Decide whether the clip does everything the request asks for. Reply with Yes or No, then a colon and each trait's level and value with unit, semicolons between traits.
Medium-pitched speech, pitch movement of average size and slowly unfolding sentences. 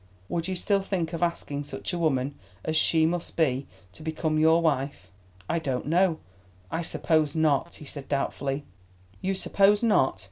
No: medium, 160 Hz; average, 3.2 semitones; average, 170 wpm